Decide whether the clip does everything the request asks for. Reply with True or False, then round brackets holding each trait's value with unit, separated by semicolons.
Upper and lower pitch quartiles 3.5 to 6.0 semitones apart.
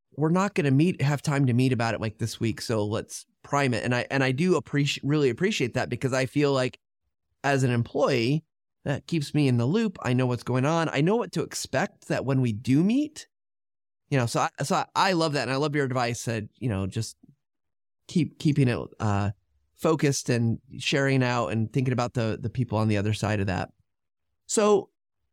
True (4.5 semitones)